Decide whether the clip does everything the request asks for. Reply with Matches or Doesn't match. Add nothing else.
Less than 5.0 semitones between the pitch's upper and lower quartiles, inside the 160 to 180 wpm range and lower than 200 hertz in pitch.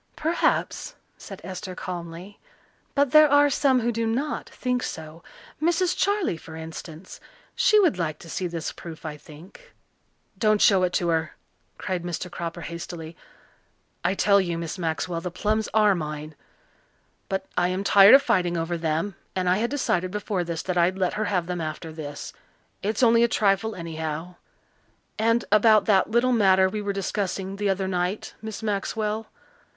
Matches